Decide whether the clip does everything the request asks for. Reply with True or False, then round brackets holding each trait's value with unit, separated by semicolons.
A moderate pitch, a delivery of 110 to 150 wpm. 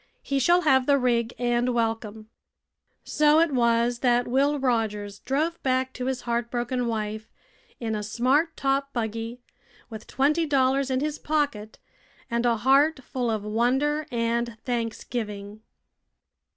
False (245 Hz; 140 wpm)